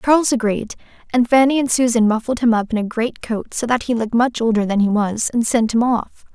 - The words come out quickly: Yes, fast, 235 wpm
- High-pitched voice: Yes, high, 230 Hz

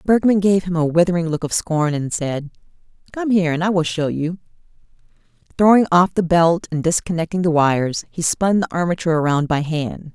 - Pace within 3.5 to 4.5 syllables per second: No, 5.6 syllables/s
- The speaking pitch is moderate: Yes, medium, 170 Hz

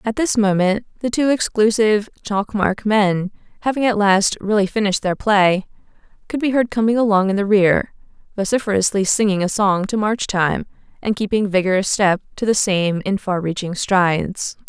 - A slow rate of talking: No, average, 170 wpm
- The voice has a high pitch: Yes, high, 205 Hz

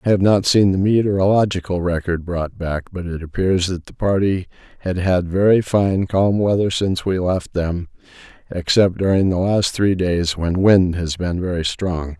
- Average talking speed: Yes, average, 180 wpm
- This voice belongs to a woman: No, male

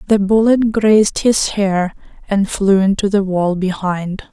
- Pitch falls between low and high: No, high, 200 Hz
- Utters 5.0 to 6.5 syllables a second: No, 4.0 syllables/s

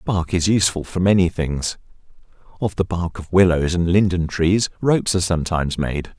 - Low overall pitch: Yes, very low, 90 Hz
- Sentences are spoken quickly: No, average, 175 wpm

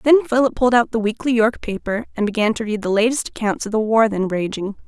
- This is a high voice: Yes, high, 225 Hz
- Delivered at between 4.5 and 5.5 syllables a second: No, 6.1 syllables/s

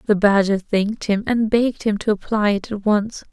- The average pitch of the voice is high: Yes, high, 210 Hz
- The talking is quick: Yes, fast, 215 wpm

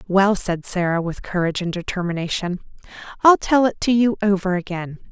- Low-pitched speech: No, high, 190 Hz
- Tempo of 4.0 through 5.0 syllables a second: No, 5.5 syllables/s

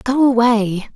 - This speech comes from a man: No, female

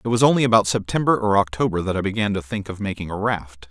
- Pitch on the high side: No, low, 105 Hz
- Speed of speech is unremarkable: No, fast, 260 wpm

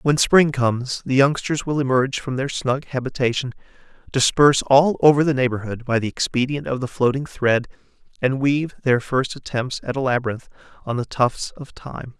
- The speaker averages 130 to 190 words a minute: Yes, average, 175 wpm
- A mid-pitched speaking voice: No, low, 130 Hz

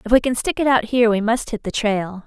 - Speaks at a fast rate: Yes, fast, 320 wpm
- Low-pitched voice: No, high, 230 Hz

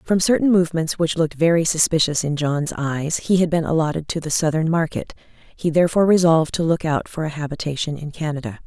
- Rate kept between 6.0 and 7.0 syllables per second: Yes, 6.1 syllables/s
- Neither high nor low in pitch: Yes, medium, 160 Hz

